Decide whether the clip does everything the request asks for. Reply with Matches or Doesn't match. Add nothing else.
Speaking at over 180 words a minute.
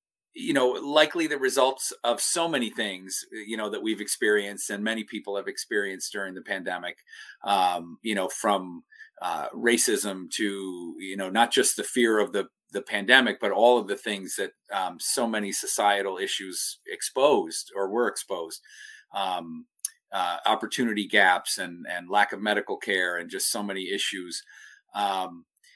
Doesn't match